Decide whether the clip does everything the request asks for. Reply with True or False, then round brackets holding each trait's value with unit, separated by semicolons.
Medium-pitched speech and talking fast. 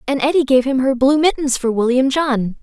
False (265 Hz; 230 wpm)